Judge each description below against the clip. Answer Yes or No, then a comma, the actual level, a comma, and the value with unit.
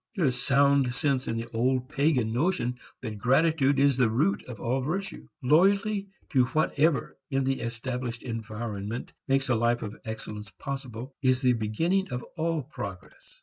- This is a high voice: No, low, 130 Hz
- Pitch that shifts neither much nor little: Yes, average, 3.5 semitones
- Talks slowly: No, average, 160 wpm